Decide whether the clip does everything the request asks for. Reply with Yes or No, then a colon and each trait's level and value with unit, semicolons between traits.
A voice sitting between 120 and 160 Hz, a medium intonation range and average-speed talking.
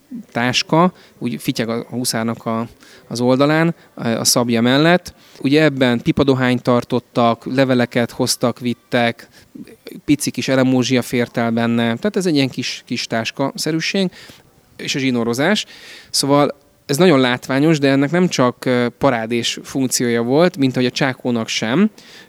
Yes: low, 130 Hz; average, 3.6 semitones; average, 135 wpm